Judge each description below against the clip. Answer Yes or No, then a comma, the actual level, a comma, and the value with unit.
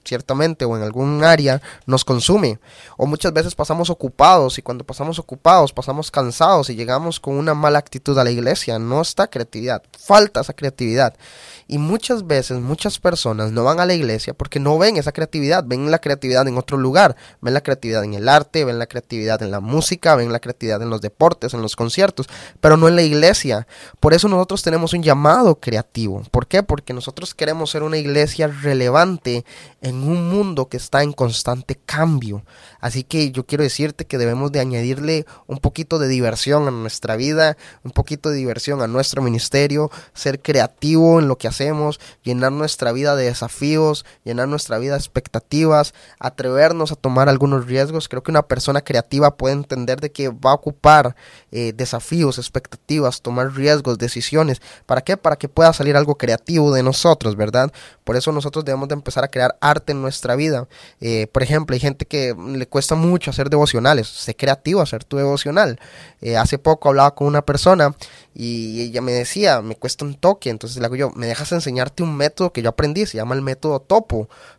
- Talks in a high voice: No, medium, 140 Hz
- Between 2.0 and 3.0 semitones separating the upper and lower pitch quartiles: No, average, 3.8 semitones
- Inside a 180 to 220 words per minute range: Yes, fast, 190 wpm